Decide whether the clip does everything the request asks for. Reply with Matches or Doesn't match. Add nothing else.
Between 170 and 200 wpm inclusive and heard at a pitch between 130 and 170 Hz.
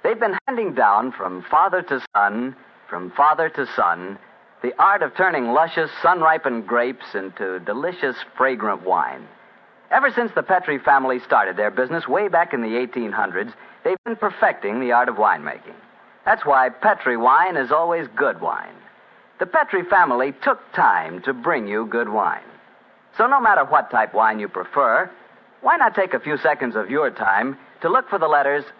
Matches